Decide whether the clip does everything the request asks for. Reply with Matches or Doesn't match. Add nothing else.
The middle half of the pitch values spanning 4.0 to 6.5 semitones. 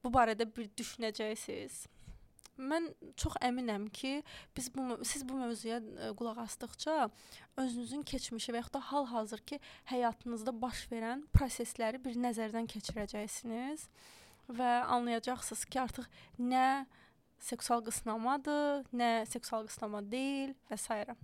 Doesn't match